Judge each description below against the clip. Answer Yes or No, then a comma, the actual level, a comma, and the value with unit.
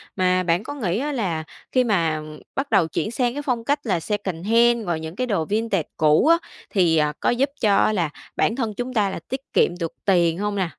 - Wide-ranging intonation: Yes, wide, 5.9 semitones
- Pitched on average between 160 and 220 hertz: Yes, high, 200 Hz